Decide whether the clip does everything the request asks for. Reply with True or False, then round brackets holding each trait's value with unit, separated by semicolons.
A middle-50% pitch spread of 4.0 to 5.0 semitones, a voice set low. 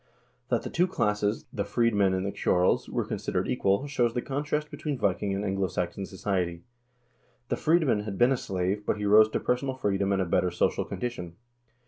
True (4.4 semitones; 105 Hz)